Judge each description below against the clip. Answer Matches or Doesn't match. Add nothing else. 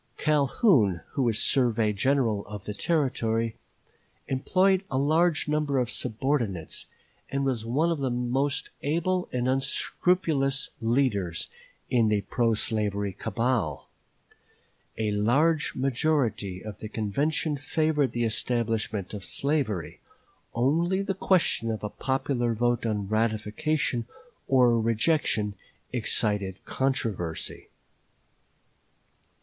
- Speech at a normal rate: Doesn't match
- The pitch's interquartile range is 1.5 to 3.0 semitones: Doesn't match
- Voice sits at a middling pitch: Doesn't match